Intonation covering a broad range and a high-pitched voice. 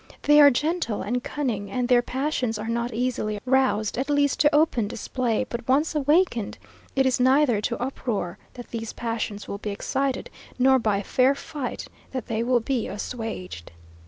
No: average, 3.3 semitones; high, 245 Hz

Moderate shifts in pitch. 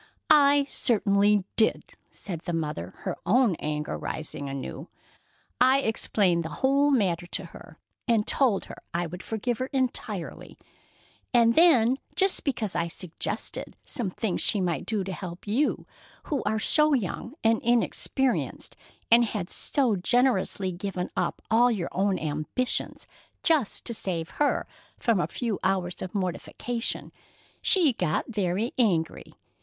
No: wide, 5.7 semitones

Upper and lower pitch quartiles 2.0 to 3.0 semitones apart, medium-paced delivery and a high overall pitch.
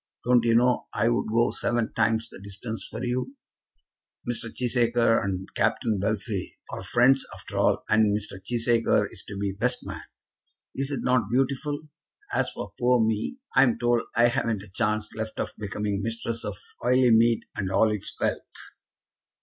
No: narrow, 2.5 semitones; average, 165 wpm; low, 115 Hz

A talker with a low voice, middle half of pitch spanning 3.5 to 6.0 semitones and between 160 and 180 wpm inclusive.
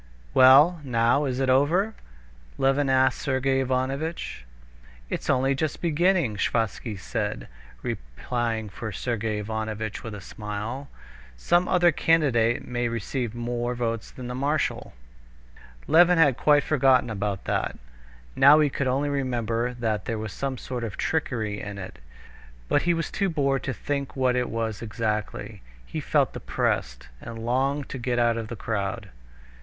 No: low, 125 Hz; average, 3.9 semitones; average, 150 wpm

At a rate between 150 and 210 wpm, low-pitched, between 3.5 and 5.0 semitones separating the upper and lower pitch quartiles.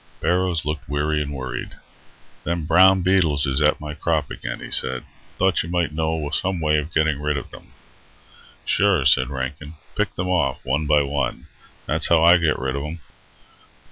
No: average, 180 wpm; very low, 75 Hz; average, 2.8 semitones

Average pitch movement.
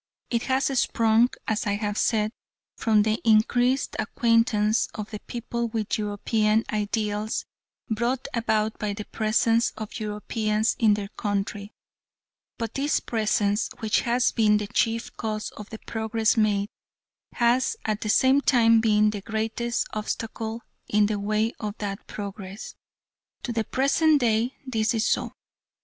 No: narrow, 1.7 semitones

